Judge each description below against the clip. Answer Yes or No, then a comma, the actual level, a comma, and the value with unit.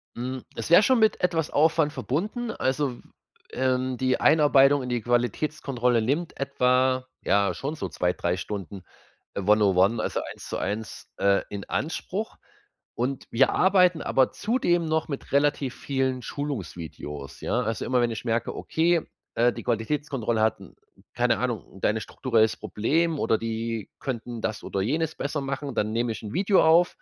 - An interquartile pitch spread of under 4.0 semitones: No, average, 5.1 semitones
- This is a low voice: Yes, low, 130 Hz